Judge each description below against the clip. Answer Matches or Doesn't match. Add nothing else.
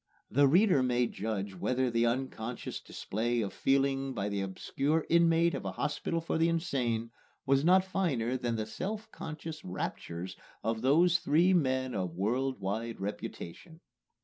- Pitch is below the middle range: Matches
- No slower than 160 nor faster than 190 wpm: Doesn't match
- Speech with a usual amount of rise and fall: Doesn't match